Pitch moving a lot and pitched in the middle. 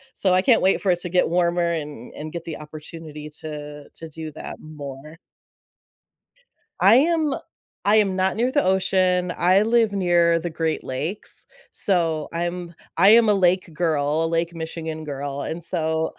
No: average, 3.1 semitones; medium, 170 Hz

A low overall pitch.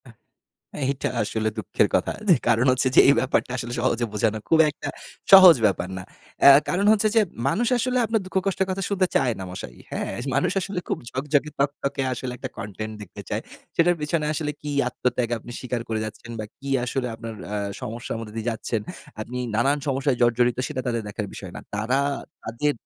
Yes: low, 125 Hz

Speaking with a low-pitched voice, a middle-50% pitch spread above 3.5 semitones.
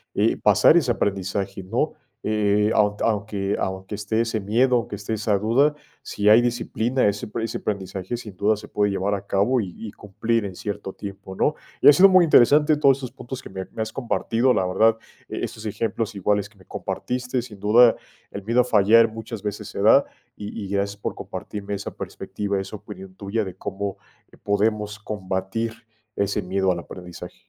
No: low, 105 Hz; narrow, 2.5 semitones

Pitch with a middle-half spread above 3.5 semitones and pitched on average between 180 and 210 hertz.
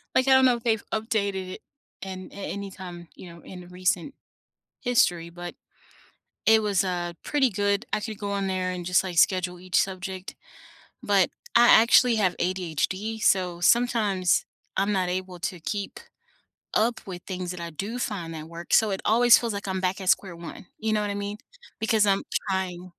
No: average, 3.1 semitones; high, 190 Hz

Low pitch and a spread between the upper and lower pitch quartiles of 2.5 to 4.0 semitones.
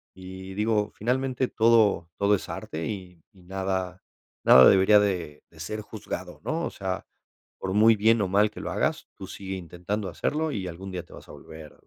Yes: very low, 95 Hz; average, 2.8 semitones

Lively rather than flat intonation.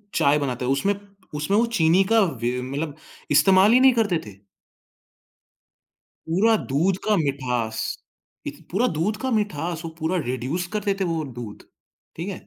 Yes: wide, 6.6 semitones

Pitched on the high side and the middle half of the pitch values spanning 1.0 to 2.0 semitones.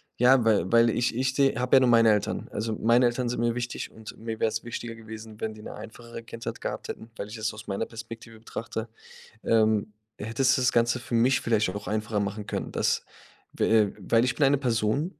No: low, 115 Hz; narrow, 1.7 semitones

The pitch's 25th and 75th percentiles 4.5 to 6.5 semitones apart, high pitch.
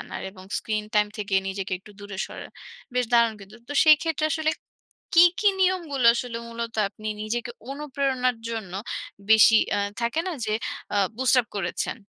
Yes: average, 4.8 semitones; high, 235 Hz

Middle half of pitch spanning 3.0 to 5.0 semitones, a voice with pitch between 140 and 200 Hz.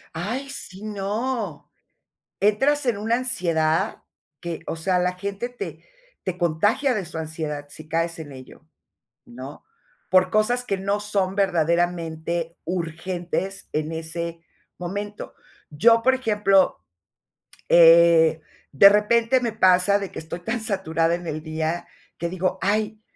Yes: average, 4.2 semitones; medium, 185 Hz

